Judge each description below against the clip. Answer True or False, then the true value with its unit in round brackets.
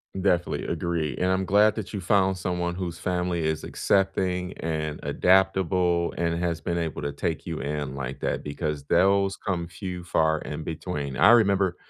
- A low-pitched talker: True (85 Hz)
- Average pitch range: True (3.0 semitones)